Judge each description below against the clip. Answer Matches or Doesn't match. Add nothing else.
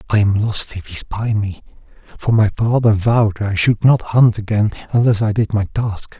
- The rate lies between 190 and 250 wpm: Matches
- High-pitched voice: Doesn't match